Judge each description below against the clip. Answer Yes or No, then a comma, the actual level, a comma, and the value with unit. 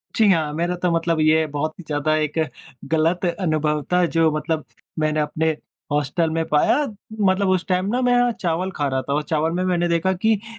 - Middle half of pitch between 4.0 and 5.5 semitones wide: No, average, 2.8 semitones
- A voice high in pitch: No, medium, 165 Hz